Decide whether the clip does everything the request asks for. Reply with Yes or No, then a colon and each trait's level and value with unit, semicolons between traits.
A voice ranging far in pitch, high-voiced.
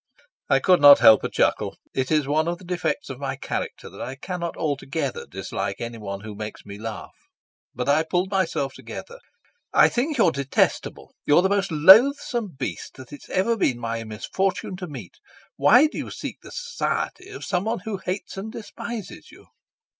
No: wide, 7.5 semitones; medium, 170 Hz